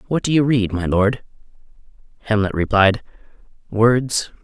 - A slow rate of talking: Yes, slow, 120 wpm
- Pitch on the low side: Yes, low, 110 Hz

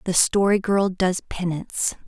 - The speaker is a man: No, female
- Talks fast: No, average, 145 wpm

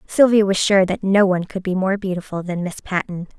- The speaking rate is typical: No, fast, 230 wpm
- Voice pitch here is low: No, high, 190 Hz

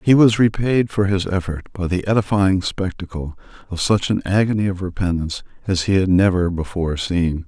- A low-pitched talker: Yes, very low, 95 Hz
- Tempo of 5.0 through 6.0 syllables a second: Yes, 5.4 syllables/s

